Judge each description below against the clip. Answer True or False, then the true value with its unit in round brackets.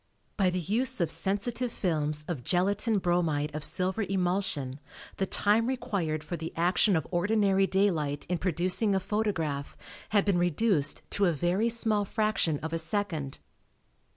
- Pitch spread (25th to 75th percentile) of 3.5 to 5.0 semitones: True (4.1 semitones)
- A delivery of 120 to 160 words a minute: True (155 wpm)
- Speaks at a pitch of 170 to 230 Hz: True (185 Hz)